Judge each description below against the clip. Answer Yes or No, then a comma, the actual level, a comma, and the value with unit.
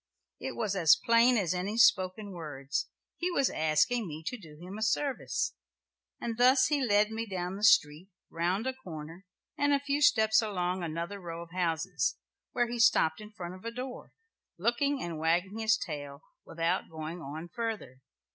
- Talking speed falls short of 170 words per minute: No, average, 175 wpm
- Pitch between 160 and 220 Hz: Yes, high, 190 Hz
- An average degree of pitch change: No, wide, 5.8 semitones